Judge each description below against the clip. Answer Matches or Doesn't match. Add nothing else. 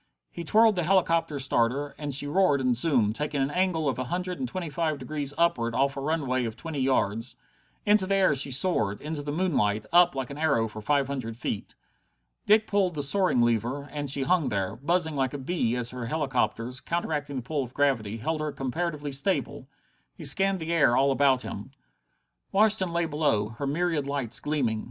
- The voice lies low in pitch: Doesn't match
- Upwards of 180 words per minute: Matches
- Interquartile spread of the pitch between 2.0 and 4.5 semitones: Doesn't match